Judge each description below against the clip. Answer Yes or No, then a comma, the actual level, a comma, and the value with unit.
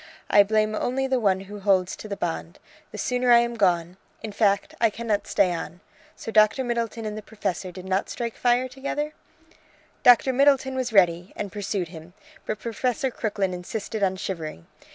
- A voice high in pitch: Yes, high, 215 Hz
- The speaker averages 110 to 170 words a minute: No, average, 180 wpm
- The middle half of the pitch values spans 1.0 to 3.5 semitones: No, average, 4.1 semitones